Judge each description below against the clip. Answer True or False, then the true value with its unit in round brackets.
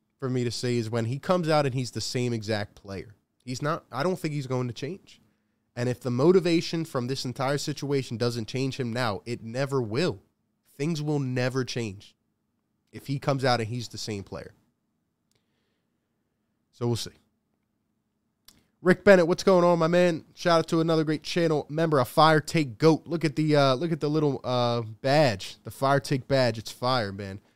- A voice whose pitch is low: True (130 Hz)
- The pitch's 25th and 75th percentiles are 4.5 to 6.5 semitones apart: True (5.3 semitones)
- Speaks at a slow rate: False (195 wpm)